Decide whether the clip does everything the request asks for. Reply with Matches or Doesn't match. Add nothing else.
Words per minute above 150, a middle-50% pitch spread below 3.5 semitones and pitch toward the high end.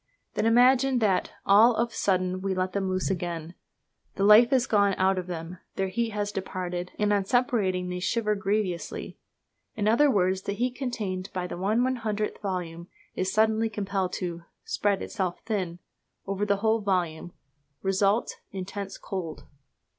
Matches